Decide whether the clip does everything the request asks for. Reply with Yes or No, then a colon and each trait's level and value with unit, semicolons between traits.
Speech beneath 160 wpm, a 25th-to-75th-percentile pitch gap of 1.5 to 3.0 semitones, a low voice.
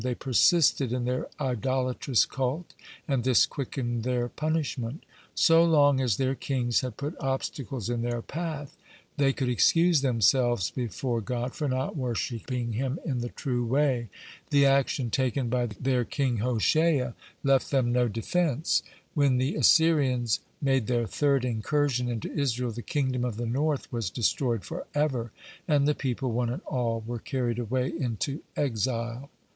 Yes: average, 150 wpm; narrow, 2.6 semitones; low, 125 Hz